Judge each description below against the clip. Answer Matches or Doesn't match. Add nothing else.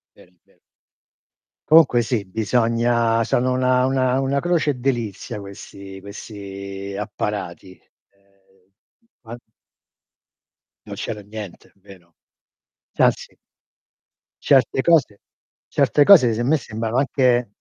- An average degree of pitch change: Matches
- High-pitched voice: Doesn't match